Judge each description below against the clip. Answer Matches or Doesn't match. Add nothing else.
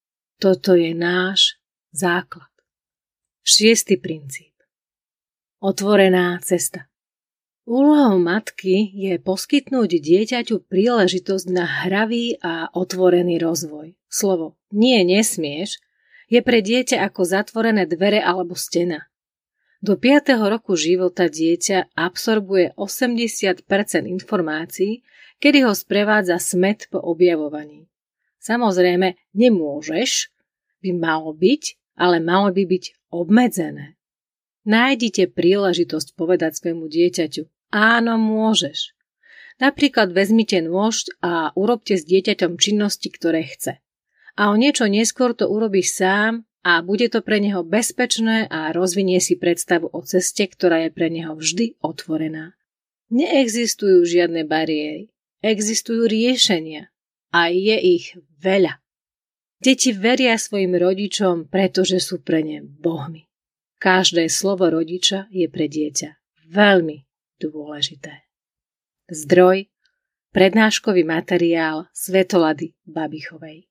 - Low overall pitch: Doesn't match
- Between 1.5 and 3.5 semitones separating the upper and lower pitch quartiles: Doesn't match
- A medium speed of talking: Doesn't match